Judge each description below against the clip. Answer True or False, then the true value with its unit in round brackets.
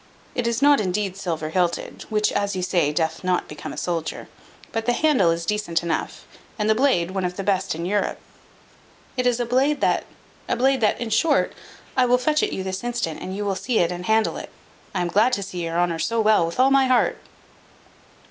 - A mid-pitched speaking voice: False (200 Hz)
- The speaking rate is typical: False (225 wpm)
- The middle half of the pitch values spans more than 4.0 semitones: True (5.5 semitones)